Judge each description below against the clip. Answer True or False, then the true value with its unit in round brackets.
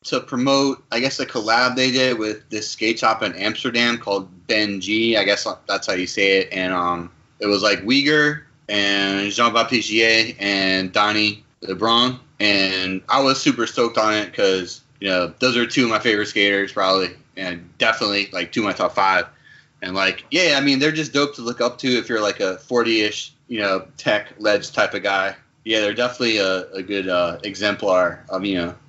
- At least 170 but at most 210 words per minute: True (200 wpm)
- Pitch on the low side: True (110 Hz)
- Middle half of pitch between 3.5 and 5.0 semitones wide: True (4.1 semitones)